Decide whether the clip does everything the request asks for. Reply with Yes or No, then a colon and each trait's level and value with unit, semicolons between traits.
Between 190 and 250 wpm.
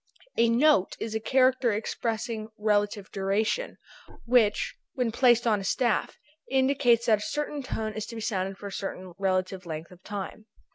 No: average, 170 wpm